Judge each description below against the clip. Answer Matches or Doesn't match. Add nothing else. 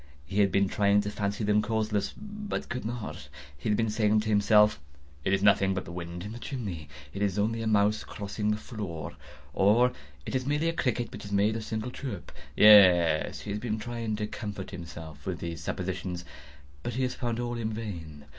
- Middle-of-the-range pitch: Doesn't match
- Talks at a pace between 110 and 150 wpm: Doesn't match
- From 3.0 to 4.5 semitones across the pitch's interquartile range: Matches